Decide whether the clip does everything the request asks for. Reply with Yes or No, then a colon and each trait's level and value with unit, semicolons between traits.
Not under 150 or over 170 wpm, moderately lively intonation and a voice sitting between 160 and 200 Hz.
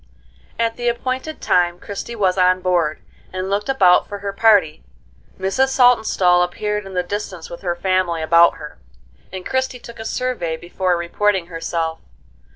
Yes: average, 160 wpm; average, 4.2 semitones; high, 190 Hz